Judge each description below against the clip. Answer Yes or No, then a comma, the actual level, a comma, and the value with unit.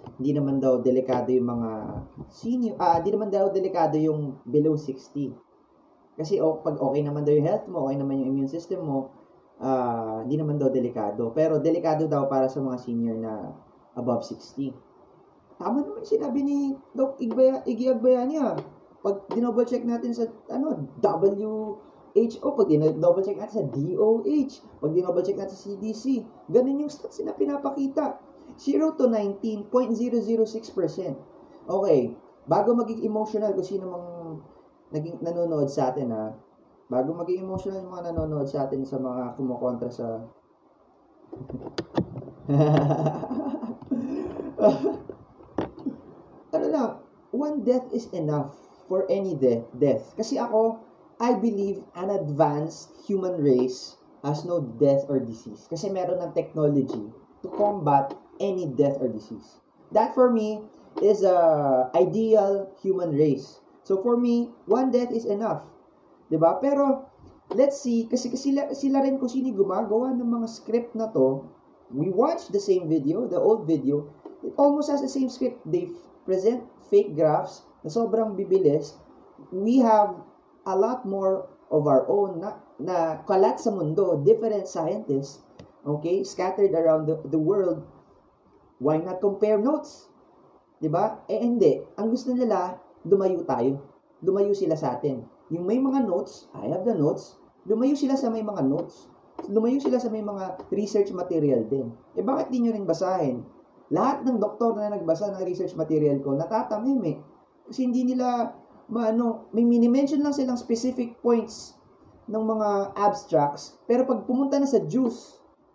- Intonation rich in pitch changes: Yes, wide, 7.8 semitones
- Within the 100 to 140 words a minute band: No, average, 150 wpm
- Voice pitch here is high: Yes, high, 200 Hz